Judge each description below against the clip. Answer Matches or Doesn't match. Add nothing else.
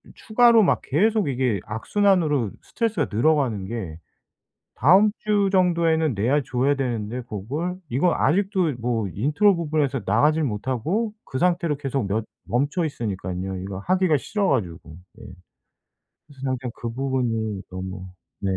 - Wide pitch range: Matches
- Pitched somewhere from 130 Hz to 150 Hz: Matches